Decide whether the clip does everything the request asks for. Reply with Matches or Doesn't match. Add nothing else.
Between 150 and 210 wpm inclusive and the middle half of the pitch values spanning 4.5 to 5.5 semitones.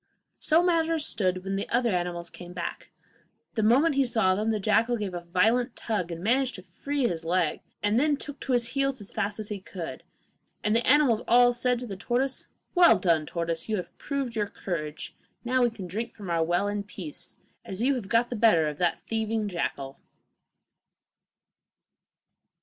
Matches